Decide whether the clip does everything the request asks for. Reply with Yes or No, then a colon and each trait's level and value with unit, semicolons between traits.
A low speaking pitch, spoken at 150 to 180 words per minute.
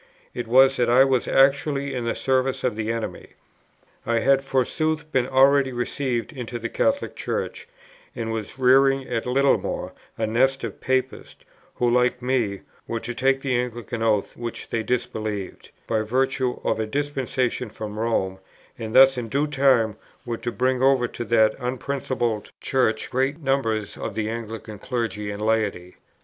Yes: low, 125 Hz; average, 160 wpm